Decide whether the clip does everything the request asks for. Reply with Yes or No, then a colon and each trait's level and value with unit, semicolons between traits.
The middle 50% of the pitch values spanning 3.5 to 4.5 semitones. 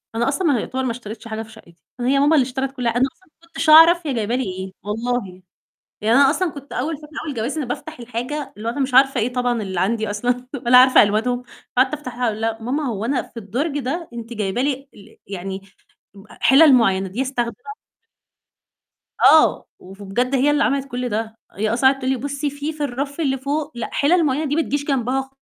Yes: average, 3.9 semitones